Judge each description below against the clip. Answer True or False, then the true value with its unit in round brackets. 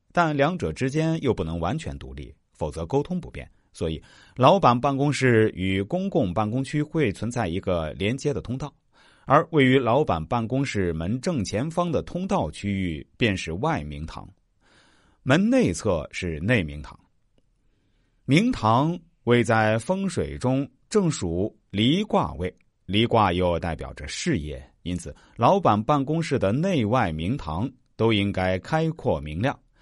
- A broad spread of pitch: True (7.5 semitones)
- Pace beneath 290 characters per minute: True (220 characters per minute)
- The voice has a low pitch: True (115 Hz)